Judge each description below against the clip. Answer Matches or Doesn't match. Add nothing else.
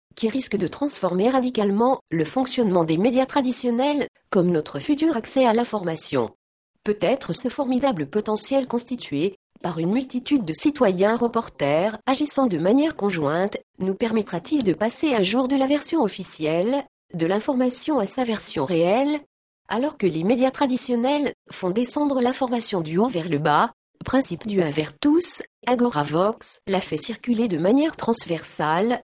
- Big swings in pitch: Matches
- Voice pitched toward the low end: Doesn't match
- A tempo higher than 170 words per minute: Doesn't match